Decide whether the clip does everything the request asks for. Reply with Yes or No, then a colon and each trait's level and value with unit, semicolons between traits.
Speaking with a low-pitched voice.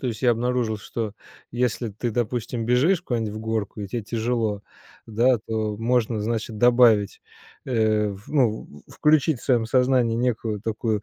Yes: low, 115 Hz